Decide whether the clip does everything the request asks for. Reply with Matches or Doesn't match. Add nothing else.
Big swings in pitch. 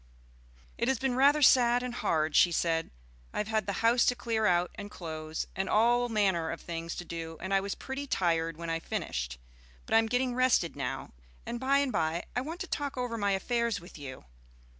Matches